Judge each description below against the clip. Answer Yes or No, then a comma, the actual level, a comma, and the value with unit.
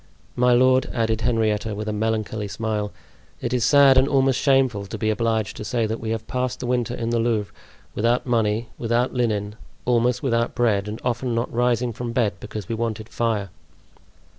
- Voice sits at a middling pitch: No, low, 115 Hz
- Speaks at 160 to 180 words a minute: No, average, 190 wpm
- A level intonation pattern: Yes, narrow, 2.2 semitones